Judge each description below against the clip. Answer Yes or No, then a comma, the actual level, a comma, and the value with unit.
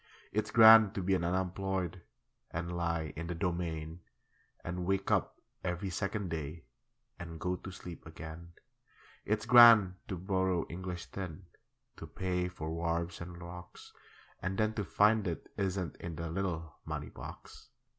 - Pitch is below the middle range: Yes, very low, 90 Hz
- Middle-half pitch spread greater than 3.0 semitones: No, narrow, 2.4 semitones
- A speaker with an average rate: Yes, average, 150 wpm